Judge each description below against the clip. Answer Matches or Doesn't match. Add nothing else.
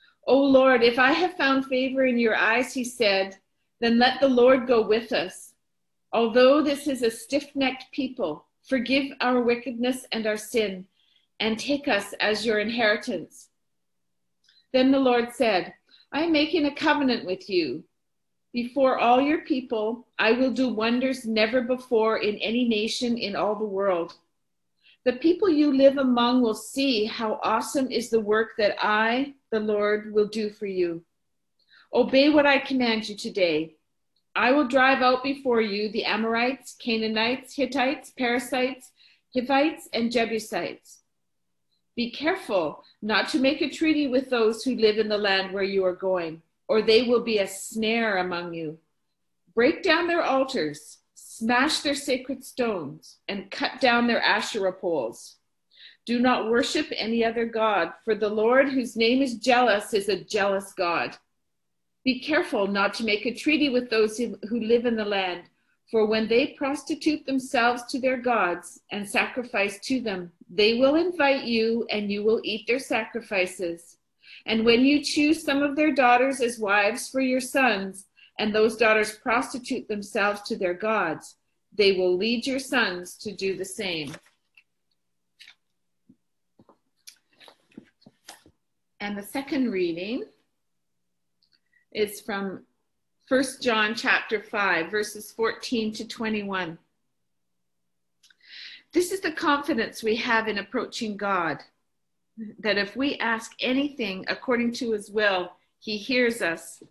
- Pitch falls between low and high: Doesn't match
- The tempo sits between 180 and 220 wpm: Doesn't match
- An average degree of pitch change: Matches